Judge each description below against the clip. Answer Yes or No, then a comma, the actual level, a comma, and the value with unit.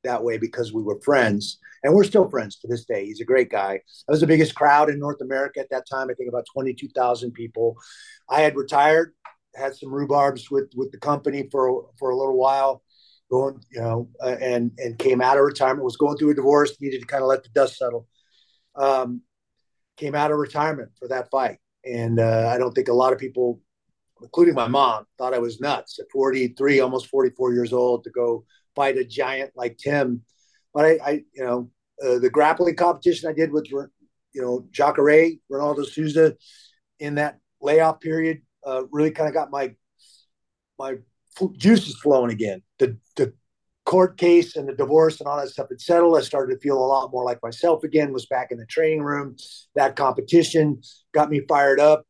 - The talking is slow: No, average, 200 wpm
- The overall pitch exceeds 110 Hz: Yes, low, 135 Hz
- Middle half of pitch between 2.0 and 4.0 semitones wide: Yes, average, 3.4 semitones